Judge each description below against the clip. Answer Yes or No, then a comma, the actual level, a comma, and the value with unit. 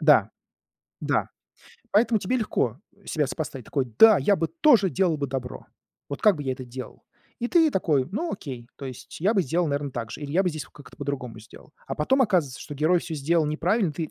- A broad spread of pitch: Yes, wide, 6.1 semitones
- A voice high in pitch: No, medium, 155 Hz